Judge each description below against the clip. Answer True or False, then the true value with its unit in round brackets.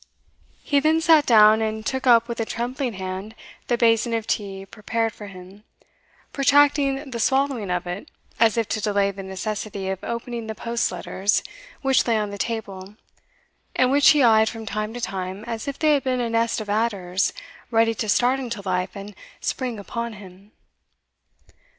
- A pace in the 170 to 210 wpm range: True (180 wpm)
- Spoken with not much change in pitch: False (3.4 semitones)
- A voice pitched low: False (225 Hz)